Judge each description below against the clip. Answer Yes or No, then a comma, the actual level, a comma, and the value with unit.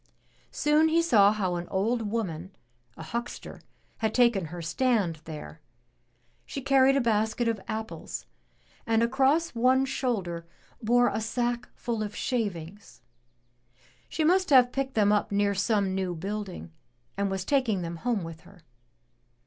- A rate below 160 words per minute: Yes, average, 145 wpm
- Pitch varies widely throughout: No, average, 4.6 semitones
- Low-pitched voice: No, high, 220 Hz